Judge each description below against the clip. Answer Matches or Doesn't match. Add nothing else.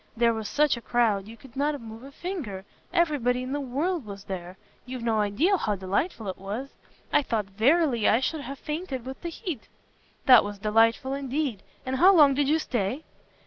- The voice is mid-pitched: Doesn't match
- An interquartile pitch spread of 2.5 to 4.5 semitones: Doesn't match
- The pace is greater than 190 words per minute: Matches